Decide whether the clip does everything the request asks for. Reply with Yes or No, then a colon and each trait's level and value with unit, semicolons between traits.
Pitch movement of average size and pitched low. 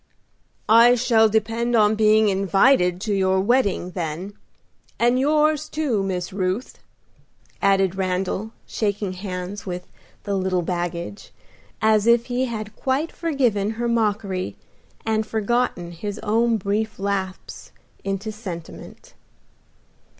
No: average, 3.6 semitones; high, 210 Hz